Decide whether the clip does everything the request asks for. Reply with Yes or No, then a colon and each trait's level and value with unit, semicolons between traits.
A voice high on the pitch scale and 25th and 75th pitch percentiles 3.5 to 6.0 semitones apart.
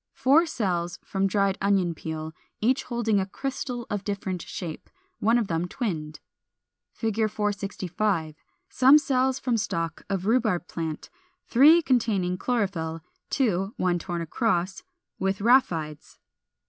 Yes: high, 200 Hz; average, 5.2 semitones